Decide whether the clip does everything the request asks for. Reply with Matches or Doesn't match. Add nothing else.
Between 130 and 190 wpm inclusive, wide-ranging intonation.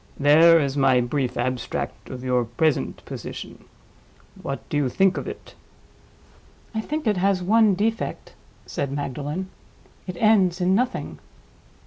Matches